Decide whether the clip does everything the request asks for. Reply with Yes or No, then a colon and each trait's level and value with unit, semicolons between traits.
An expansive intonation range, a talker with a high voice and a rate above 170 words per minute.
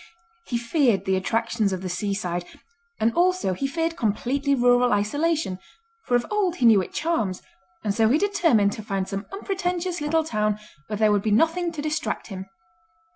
Yes: wide, 8.0 semitones; high, 235 Hz; average, 180 wpm